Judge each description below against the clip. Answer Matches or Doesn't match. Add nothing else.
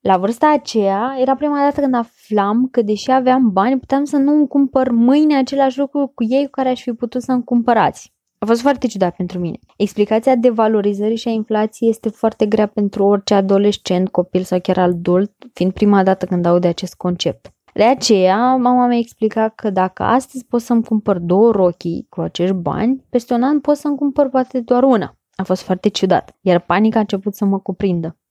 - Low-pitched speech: Doesn't match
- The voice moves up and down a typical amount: Matches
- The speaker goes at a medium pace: Doesn't match